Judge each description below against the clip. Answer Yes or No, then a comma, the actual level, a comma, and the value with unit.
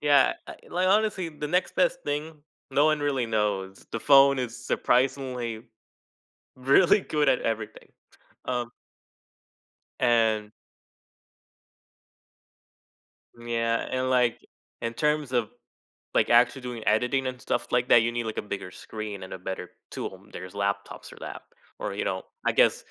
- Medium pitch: No, low, 120 Hz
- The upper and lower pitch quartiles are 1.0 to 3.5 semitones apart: No, average, 4.0 semitones